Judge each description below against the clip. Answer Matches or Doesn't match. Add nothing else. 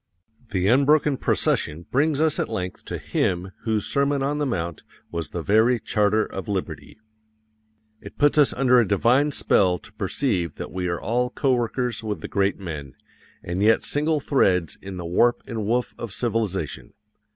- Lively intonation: Matches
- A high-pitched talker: Doesn't match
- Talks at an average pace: Matches